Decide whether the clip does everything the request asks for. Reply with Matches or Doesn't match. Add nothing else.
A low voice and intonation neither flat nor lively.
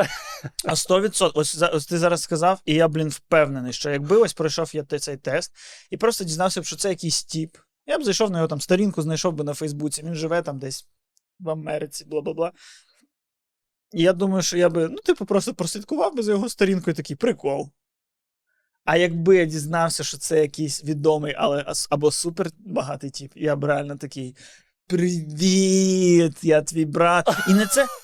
Doesn't match